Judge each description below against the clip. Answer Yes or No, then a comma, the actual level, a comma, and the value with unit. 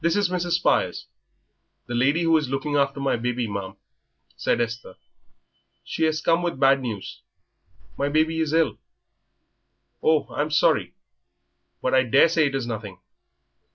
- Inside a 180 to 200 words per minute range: No, average, 150 wpm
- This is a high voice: No, medium, 140 Hz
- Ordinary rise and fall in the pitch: Yes, average, 4.8 semitones